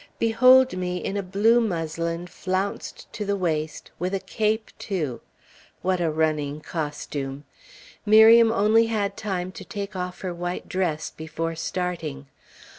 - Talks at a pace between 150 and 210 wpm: No, average, 140 wpm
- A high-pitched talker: No, medium, 180 Hz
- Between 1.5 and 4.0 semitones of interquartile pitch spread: No, average, 4.4 semitones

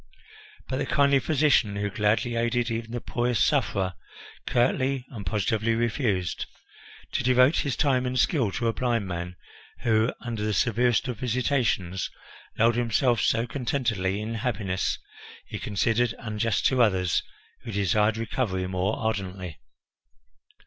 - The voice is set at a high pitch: No, low, 115 Hz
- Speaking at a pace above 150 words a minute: No, slow, 135 wpm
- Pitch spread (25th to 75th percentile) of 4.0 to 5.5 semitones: No, average, 3.5 semitones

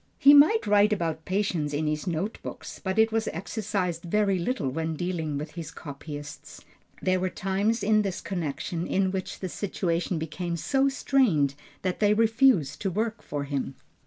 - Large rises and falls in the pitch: No, average, 4.7 semitones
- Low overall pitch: No, medium, 185 Hz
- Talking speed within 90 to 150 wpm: No, average, 170 wpm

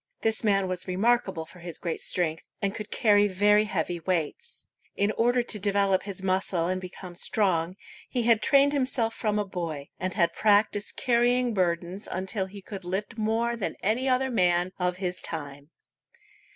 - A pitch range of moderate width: Yes, average, 3.6 semitones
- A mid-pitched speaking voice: No, high, 195 Hz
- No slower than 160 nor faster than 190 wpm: Yes, average, 170 wpm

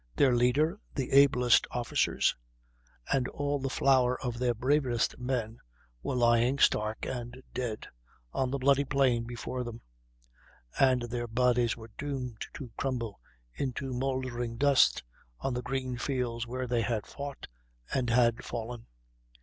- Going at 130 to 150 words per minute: Yes, average, 140 wpm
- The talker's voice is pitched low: Yes, low, 125 Hz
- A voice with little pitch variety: Yes, narrow, 2.1 semitones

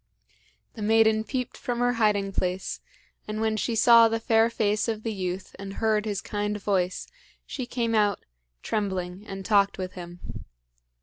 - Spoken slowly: No, average, 165 wpm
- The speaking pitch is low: No, high, 210 Hz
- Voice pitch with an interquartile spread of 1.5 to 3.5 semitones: Yes, narrow, 2.4 semitones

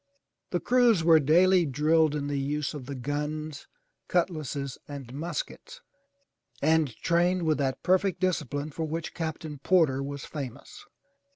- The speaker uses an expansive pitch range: No, average, 3.4 semitones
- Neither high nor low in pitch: Yes, medium, 155 Hz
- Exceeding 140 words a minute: No, slow, 135 wpm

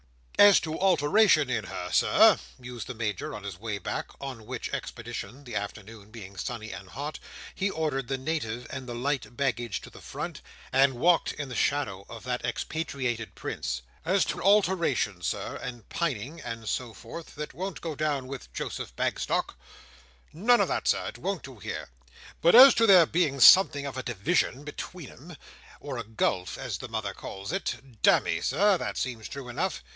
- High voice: No, low, 130 Hz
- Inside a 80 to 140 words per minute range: No, average, 175 wpm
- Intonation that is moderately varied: No, wide, 5.9 semitones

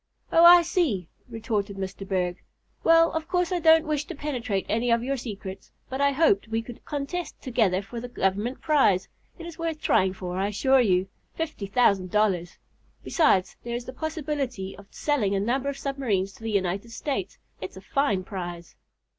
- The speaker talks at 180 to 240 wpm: Yes, average, 185 wpm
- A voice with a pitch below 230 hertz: No, high, 235 Hz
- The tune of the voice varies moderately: No, wide, 7.0 semitones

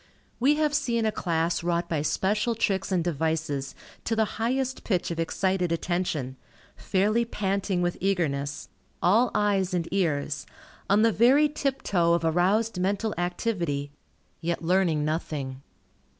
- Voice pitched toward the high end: No, medium, 180 Hz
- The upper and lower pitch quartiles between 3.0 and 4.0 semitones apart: No, average, 4.8 semitones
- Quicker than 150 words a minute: No, slow, 135 wpm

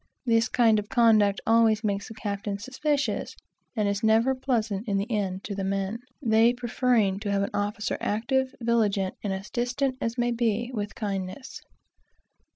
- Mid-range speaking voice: No, high, 220 Hz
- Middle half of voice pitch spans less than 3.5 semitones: Yes, average, 2.9 semitones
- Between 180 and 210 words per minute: No, average, 160 wpm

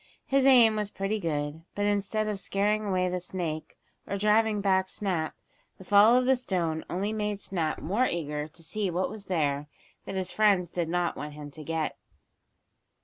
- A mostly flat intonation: No, average, 4.3 semitones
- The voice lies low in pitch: No, high, 190 Hz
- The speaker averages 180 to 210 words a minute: Yes, average, 185 wpm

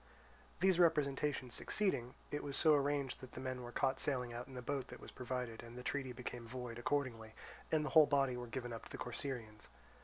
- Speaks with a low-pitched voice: Yes, low, 130 Hz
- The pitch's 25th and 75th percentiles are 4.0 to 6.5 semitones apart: No, average, 2.7 semitones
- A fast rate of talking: Yes, fast, 215 wpm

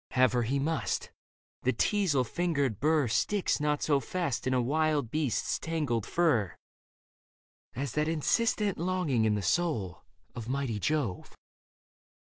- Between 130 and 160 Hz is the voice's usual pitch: Yes, medium, 140 Hz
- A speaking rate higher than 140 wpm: No, slow, 135 wpm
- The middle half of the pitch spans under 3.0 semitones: No, average, 5.1 semitones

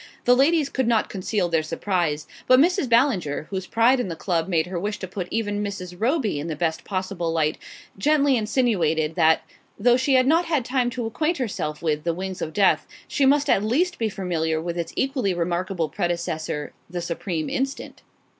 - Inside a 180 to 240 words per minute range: Yes, average, 190 wpm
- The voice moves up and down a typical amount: No, wide, 7.1 semitones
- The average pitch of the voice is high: Yes, high, 195 Hz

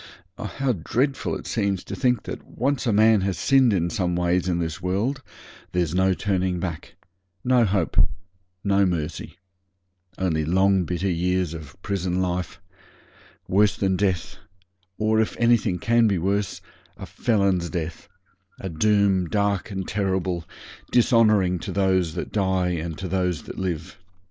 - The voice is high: No, very low, 95 Hz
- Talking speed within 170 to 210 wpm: No, average, 155 wpm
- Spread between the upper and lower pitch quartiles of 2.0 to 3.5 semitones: Yes, average, 2.7 semitones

